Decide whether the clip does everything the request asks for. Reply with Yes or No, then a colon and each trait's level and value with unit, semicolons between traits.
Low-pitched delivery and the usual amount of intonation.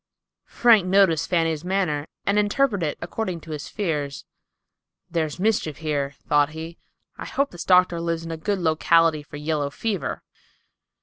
No: medium, 165 Hz; average, 3.9 semitones